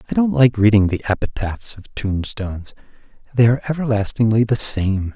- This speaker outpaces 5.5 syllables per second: No, 5.4 syllables/s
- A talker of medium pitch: No, low, 110 Hz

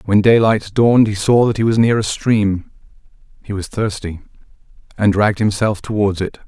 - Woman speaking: No, male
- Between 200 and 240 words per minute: No, average, 175 wpm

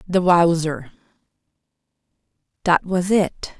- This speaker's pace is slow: Yes, slow, 85 wpm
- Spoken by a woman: Yes, female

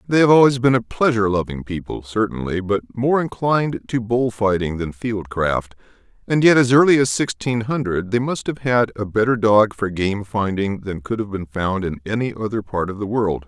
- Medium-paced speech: No, fast, 210 wpm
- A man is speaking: Yes, male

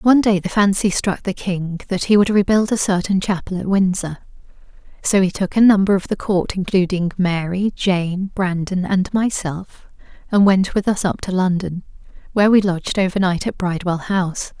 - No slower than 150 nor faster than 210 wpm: Yes, average, 185 wpm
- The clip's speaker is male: No, female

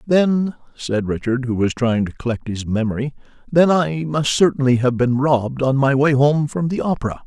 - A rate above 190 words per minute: Yes, average, 200 wpm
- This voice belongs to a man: Yes, male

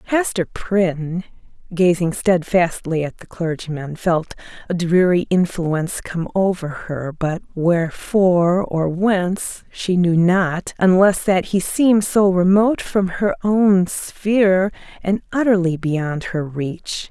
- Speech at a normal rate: No, slow, 125 wpm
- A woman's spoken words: Yes, female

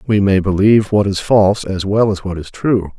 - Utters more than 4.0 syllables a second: Yes, 5.4 syllables/s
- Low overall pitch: Yes, low, 100 Hz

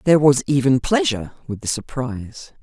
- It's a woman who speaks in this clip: Yes, female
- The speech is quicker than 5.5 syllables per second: Yes, 5.8 syllables/s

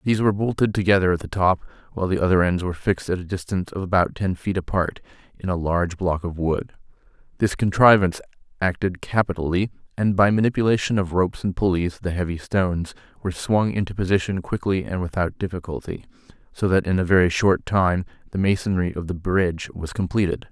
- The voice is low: Yes, very low, 95 Hz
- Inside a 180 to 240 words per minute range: Yes, average, 185 wpm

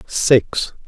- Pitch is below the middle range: Yes, low, 125 Hz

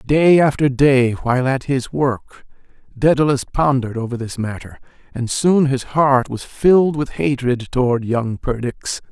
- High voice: No, low, 135 Hz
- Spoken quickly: No, average, 150 wpm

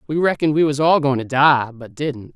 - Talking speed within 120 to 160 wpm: No, fast, 255 wpm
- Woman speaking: No, male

